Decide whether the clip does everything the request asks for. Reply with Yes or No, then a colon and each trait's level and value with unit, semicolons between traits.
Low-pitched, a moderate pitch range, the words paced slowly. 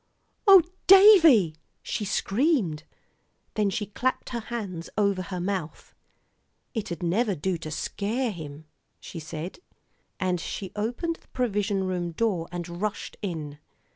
No: high, 195 Hz; average, 4.8 semitones; slow, 130 wpm